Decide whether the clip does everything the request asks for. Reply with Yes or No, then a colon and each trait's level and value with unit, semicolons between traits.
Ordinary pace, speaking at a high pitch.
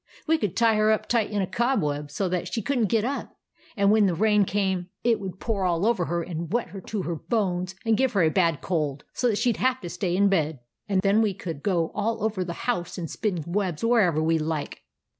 No: fast, 255 wpm; high, 195 Hz